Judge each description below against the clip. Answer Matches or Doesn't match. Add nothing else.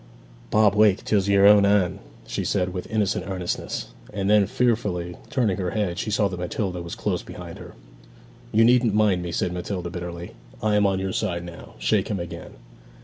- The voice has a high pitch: Doesn't match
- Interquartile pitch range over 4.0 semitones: Doesn't match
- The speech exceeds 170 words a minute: Matches